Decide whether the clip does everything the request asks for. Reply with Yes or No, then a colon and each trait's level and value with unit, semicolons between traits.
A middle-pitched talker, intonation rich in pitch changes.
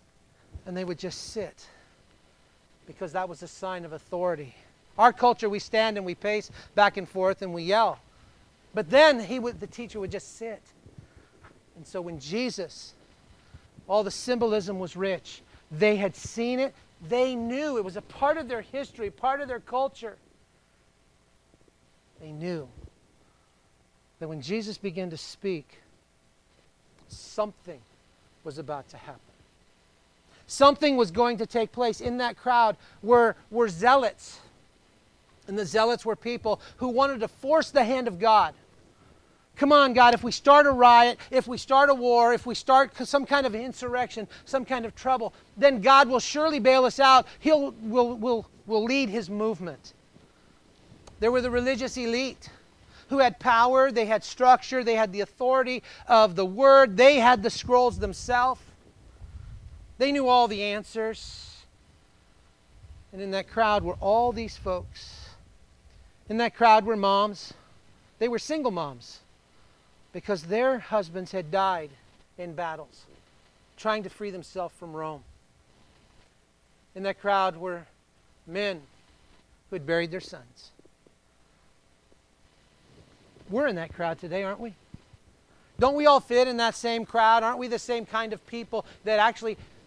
No: high, 215 Hz; wide, 6.4 semitones